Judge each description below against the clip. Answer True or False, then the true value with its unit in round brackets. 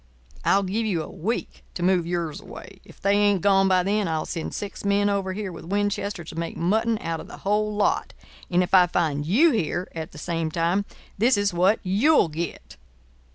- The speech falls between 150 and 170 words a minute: False (205 wpm)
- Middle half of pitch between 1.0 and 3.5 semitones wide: True (3.1 semitones)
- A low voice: False (190 Hz)